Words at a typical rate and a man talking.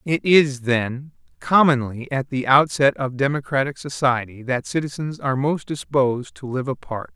Yes: average, 150 wpm; male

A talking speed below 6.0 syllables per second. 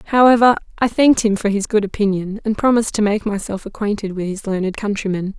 No: 6.1 syllables/s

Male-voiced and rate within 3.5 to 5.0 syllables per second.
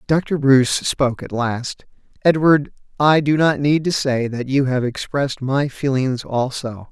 Yes: male; 4.2 syllables/s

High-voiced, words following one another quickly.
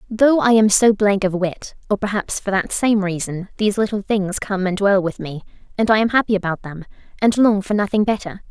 Yes: high, 200 Hz; fast, 225 wpm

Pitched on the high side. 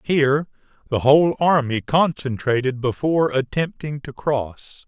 No: medium, 140 Hz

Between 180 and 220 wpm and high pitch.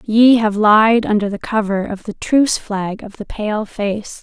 Yes: average, 200 wpm; high, 215 Hz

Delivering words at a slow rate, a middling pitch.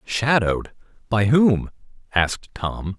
No: slow, 100 wpm; low, 110 Hz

